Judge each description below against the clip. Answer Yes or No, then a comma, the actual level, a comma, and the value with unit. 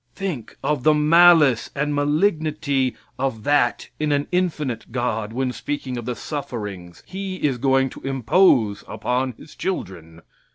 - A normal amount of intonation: Yes, average, 4.1 semitones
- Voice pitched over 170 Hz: No, low, 135 Hz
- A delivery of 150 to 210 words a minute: No, average, 140 wpm